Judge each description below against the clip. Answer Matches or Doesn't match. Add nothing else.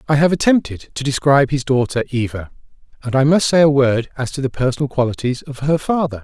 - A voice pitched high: Doesn't match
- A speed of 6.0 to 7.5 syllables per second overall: Matches